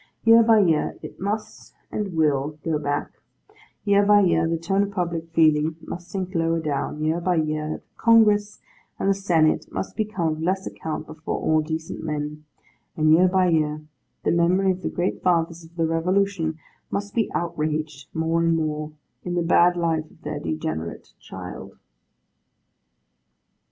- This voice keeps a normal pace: Yes, average, 165 wpm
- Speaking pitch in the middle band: Yes, medium, 165 Hz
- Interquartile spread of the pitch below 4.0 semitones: Yes, average, 3.2 semitones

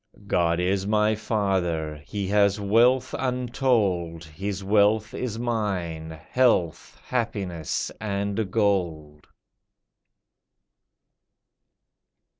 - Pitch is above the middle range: No, low, 100 Hz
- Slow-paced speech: Yes, slow, 75 wpm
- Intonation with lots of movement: No, average, 4.2 semitones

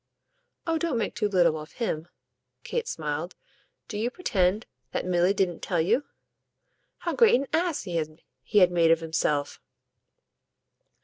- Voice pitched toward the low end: No, medium, 185 Hz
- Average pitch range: No, wide, 6.5 semitones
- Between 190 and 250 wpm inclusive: No, average, 140 wpm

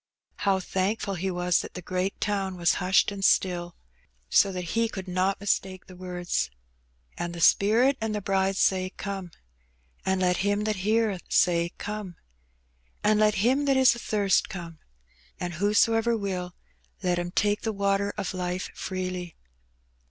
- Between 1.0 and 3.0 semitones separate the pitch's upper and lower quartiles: Yes, narrow, 2.4 semitones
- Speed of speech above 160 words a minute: Yes, average, 170 wpm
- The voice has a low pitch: No, high, 190 Hz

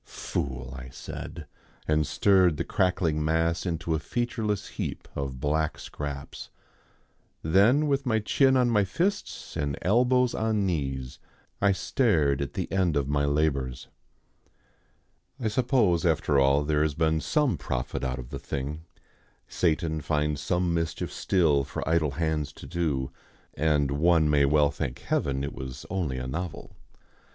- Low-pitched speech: Yes, very low, 80 Hz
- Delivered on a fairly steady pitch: No, average, 4.8 semitones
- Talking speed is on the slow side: No, average, 150 wpm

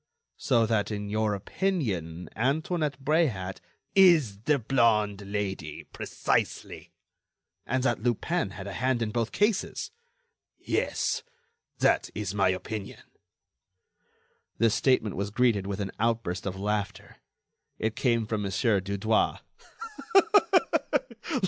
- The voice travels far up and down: No, average, 4.0 semitones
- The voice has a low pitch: Yes, low, 110 Hz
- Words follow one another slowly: Yes, slow, 110 wpm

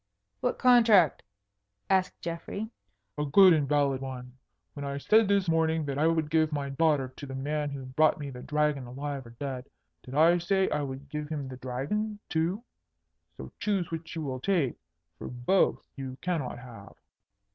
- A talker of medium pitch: Yes, medium, 150 Hz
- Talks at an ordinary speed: Yes, average, 180 wpm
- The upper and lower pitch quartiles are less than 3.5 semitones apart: No, average, 4.0 semitones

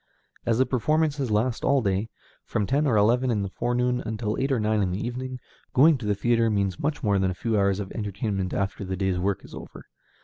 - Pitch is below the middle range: Yes, low, 110 Hz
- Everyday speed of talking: No, fast, 230 wpm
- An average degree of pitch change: Yes, average, 4.1 semitones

